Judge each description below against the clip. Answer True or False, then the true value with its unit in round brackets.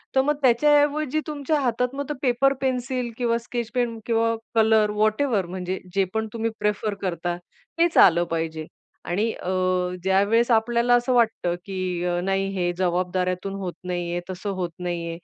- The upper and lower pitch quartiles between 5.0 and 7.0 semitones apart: True (5.3 semitones)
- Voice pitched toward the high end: True (220 Hz)